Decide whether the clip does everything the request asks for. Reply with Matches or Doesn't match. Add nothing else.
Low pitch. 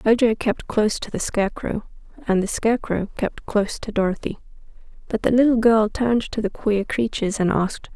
Doesn't match